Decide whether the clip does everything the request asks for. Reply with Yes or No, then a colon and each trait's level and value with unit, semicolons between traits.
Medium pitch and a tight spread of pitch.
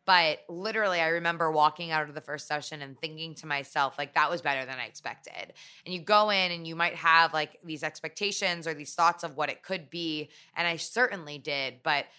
Yes: medium, 160 Hz; narrow, 2.3 semitones